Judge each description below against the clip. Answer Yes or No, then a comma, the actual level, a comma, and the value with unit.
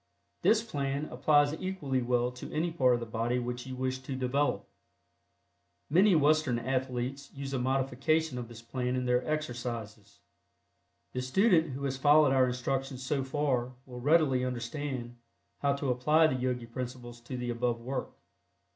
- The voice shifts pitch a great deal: No, average, 2.7 semitones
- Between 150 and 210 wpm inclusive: Yes, average, 160 wpm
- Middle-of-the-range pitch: No, low, 130 Hz